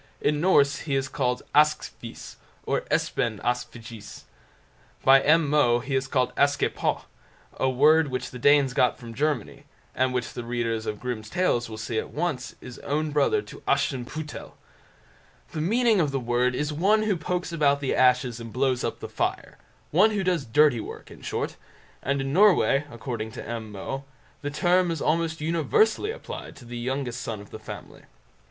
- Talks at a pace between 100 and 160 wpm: No, average, 175 wpm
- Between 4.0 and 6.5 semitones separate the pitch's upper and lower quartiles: Yes, average, 4.3 semitones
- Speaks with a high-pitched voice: No, low, 135 Hz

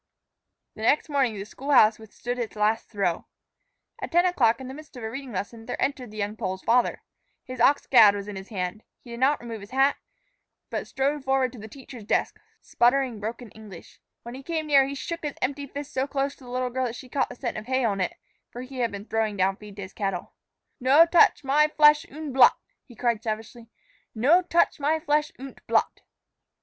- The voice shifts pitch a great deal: No, average, 4.2 semitones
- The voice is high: Yes, very high, 250 Hz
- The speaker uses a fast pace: Yes, fast, 220 wpm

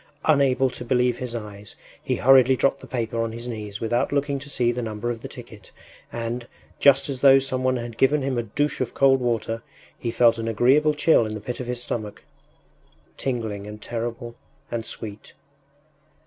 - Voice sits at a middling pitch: No, low, 120 Hz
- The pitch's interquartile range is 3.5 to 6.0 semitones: No, average, 2.7 semitones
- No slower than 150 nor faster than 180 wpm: No, average, 190 wpm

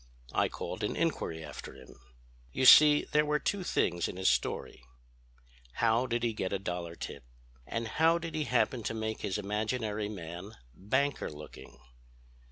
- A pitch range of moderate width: No, wide, 6.3 semitones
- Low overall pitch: Yes, low, 110 Hz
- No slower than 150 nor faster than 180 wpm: Yes, average, 165 wpm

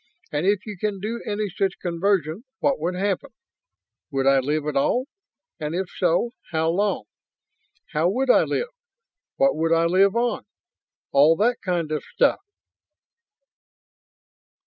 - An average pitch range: Yes, average, 4.8 semitones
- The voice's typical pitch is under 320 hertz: Yes, medium, 185 Hz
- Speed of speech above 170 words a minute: No, average, 145 wpm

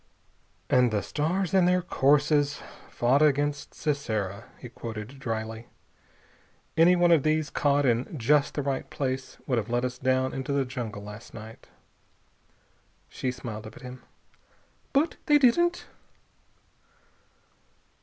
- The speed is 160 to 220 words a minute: No, slow, 135 wpm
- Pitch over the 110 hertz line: Yes, low, 135 Hz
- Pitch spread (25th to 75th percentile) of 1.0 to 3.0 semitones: No, average, 4.3 semitones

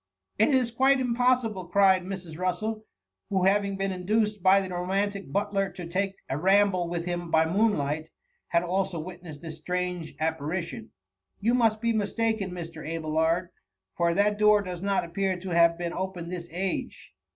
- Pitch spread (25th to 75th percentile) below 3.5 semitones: Yes, average, 3.1 semitones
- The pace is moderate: Yes, average, 180 wpm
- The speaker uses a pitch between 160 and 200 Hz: Yes, medium, 185 Hz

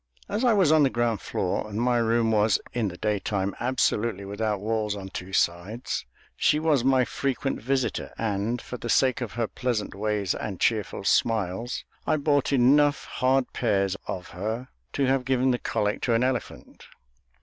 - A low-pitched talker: Yes, low, 115 Hz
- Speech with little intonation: No, average, 4.0 semitones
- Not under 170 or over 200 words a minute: Yes, average, 175 wpm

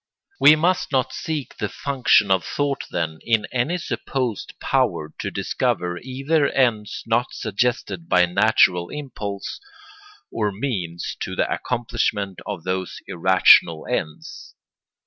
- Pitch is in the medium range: No, low, 110 Hz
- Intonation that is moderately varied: No, wide, 6.3 semitones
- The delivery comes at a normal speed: No, slow, 125 wpm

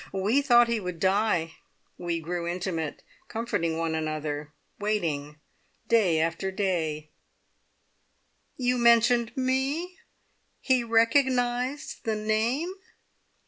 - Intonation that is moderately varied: No, wide, 6.5 semitones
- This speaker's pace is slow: Yes, slow, 100 wpm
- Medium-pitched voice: No, high, 210 Hz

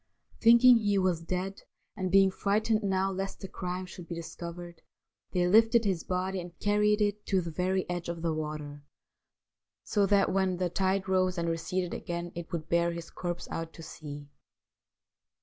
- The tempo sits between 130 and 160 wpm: No, average, 175 wpm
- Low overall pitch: No, medium, 185 Hz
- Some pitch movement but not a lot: No, narrow, 2.3 semitones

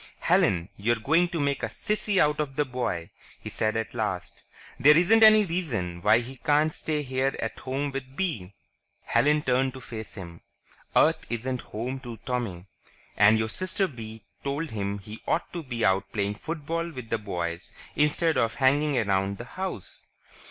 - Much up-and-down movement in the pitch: Yes, wide, 5.7 semitones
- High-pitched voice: No, low, 130 Hz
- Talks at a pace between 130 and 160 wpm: No, average, 175 wpm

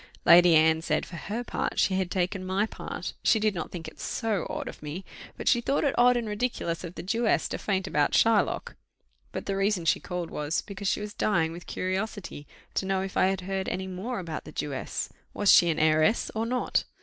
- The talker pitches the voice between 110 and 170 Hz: No, high, 190 Hz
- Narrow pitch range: No, average, 3.9 semitones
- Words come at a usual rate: No, fast, 220 wpm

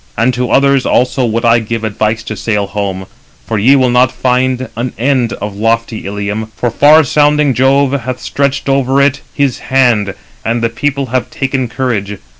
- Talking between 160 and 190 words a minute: Yes, average, 180 wpm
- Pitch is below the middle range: Yes, low, 125 Hz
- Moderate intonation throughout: Yes, average, 3.4 semitones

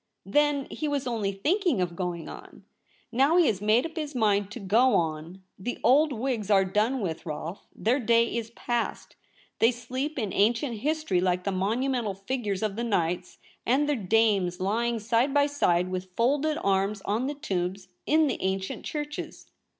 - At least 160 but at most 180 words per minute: Yes, average, 175 wpm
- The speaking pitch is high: Yes, high, 225 Hz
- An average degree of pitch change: No, wide, 5.8 semitones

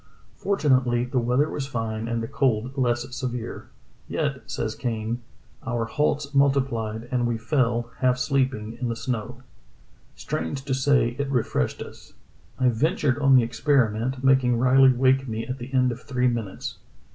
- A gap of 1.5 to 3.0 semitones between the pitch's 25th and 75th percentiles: Yes, narrow, 2.4 semitones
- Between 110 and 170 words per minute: Yes, average, 160 wpm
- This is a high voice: No, low, 125 Hz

